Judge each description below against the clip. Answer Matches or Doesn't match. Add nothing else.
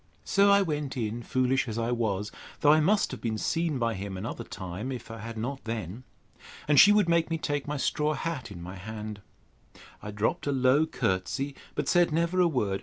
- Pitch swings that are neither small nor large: Doesn't match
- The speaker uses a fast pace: Matches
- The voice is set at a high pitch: Doesn't match